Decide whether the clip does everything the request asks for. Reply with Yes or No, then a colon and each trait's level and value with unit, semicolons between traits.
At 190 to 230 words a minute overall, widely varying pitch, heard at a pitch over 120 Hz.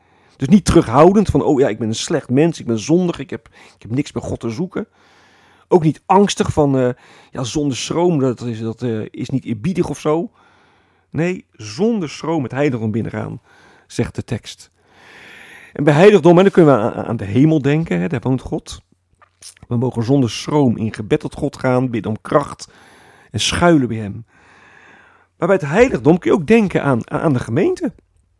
Yes: average, 195 wpm; wide, 6.4 semitones; low, 135 Hz